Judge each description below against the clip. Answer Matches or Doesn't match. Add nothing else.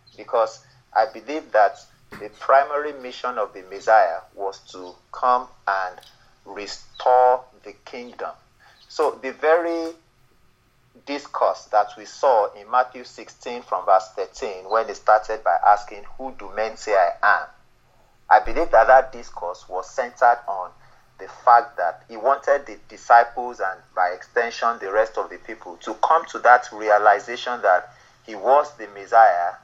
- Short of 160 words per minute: Matches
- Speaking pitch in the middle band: Doesn't match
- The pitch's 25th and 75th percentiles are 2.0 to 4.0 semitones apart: Matches